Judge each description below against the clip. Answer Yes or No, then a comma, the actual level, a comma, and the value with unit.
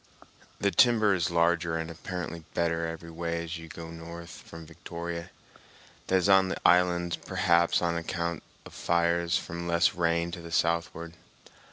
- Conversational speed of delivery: Yes, average, 160 wpm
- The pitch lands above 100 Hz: No, very low, 85 Hz